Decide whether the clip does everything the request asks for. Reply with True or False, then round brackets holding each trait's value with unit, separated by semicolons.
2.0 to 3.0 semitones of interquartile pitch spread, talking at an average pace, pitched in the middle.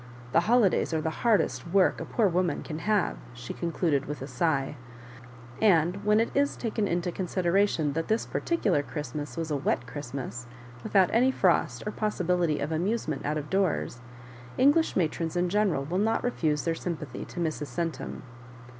False (5.1 semitones; 170 wpm; 170 Hz)